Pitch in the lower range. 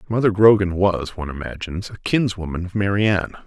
Yes: low, 100 Hz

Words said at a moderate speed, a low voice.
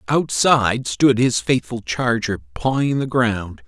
No: slow, 130 wpm; low, 120 Hz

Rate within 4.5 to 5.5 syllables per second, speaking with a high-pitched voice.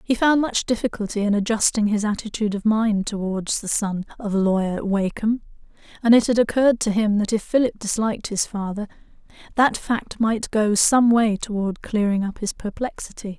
Yes: 5.2 syllables/s; high, 215 Hz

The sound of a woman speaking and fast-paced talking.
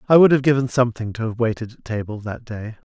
No: male; fast, 250 wpm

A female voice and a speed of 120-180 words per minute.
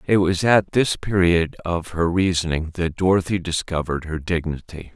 No: male; average, 155 wpm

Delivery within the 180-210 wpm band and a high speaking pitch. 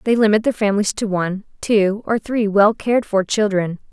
Yes: average, 200 wpm; high, 205 Hz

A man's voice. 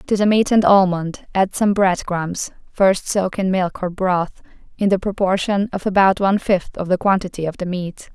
No: female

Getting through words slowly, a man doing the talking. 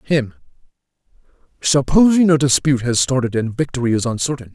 Yes: slow, 130 wpm; male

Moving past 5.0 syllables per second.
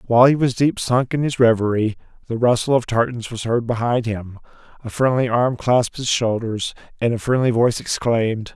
Yes: 5.4 syllables/s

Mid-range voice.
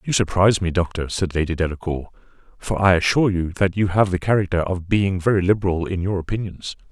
No: very low, 90 Hz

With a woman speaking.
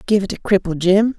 No: male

